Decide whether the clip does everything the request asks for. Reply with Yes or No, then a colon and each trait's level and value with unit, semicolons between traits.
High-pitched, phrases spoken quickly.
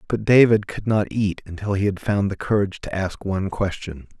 No: low, 100 Hz; fast, 215 wpm